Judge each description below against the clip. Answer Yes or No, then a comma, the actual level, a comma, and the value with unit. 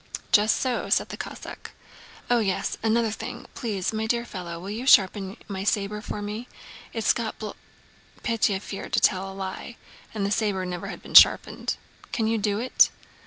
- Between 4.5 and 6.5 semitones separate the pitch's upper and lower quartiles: No, narrow, 2.6 semitones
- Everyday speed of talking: Yes, average, 180 wpm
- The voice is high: Yes, high, 210 Hz